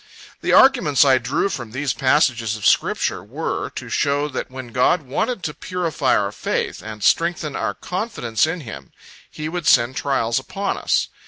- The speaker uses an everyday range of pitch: No, wide, 6.0 semitones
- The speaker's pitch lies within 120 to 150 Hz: Yes, medium, 140 Hz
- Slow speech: No, average, 170 wpm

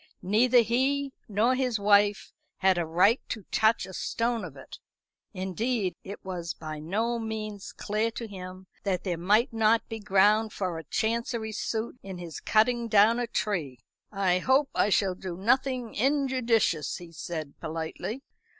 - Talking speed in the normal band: Yes, average, 160 wpm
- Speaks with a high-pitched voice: Yes, high, 210 Hz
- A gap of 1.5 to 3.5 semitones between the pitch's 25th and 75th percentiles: No, average, 4.1 semitones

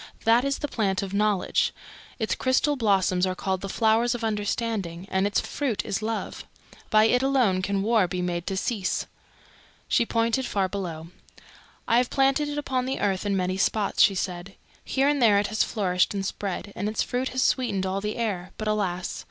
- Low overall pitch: No, high, 210 Hz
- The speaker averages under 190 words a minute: No, average, 195 wpm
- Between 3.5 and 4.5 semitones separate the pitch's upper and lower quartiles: Yes, average, 3.9 semitones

